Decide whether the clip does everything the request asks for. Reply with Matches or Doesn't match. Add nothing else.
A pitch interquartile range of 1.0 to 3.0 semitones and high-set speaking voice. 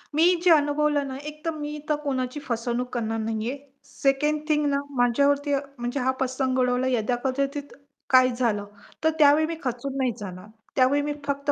Matches